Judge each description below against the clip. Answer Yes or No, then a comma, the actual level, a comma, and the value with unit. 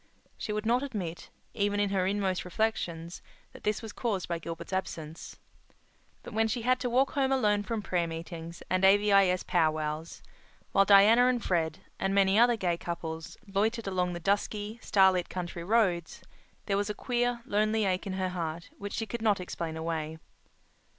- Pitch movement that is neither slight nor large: Yes, average, 4.0 semitones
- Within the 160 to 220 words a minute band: Yes, average, 175 wpm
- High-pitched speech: Yes, high, 195 Hz